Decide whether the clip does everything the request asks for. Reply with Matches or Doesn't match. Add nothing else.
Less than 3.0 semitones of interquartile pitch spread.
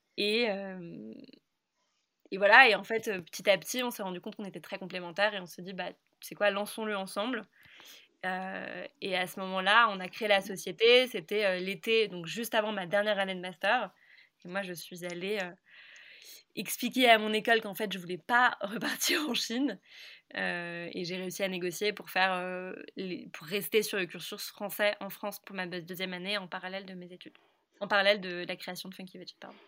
Matches